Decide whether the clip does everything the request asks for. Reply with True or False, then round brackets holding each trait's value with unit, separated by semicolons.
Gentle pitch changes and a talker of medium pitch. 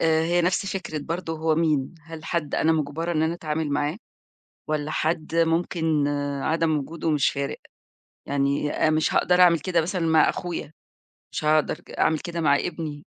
True (1.9 semitones; 160 Hz)